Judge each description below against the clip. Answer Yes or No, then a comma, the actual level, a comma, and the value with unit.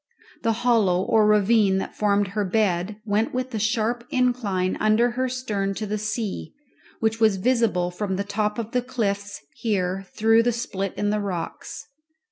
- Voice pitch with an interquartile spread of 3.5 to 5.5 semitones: No, average, 2.7 semitones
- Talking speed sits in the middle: Yes, average, 170 wpm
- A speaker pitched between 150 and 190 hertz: No, high, 215 Hz